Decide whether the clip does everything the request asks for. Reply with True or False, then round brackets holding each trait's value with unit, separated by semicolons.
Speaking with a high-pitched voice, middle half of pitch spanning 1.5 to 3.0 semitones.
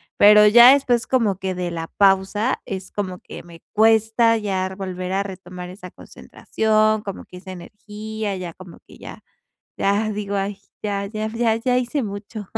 True (205 Hz; 2.6 semitones)